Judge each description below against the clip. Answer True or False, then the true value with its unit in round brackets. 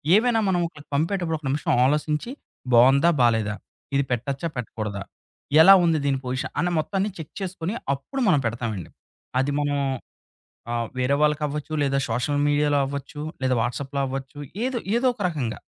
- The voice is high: False (145 Hz)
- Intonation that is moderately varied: True (4.2 semitones)